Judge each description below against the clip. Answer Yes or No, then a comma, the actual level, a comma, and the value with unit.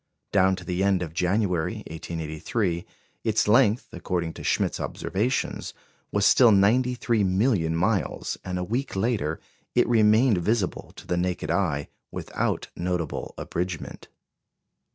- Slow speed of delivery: Yes, slow, 130 wpm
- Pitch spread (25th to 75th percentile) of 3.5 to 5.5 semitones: Yes, average, 3.9 semitones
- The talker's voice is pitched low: Yes, very low, 95 Hz